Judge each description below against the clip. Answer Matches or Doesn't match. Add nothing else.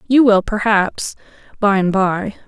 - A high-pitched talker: Matches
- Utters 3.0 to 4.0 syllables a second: Matches